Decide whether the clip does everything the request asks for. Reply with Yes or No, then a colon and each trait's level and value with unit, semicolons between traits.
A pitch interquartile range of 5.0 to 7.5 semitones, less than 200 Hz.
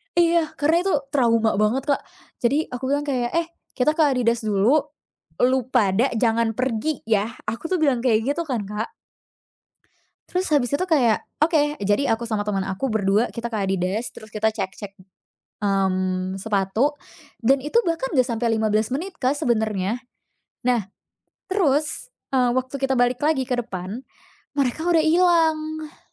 No: wide, 5.4 semitones; high, 245 Hz